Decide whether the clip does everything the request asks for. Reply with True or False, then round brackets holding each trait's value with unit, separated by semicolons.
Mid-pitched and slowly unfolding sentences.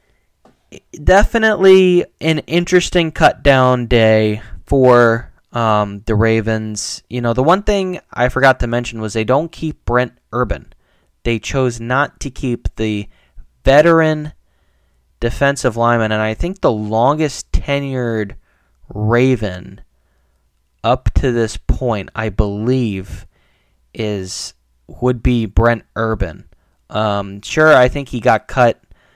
False (115 Hz; 120 wpm)